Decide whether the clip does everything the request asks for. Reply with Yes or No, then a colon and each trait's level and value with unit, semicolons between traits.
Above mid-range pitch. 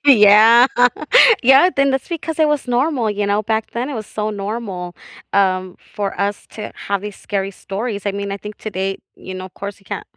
Yes: high, 210 Hz